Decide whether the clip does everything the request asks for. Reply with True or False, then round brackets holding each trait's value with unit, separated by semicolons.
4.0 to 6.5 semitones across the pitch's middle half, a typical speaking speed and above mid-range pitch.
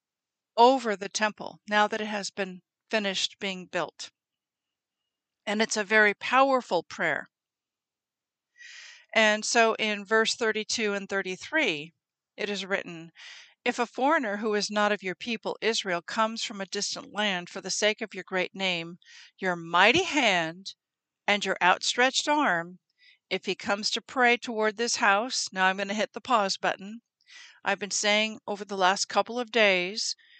False (3.4 semitones; 160 wpm; 210 Hz)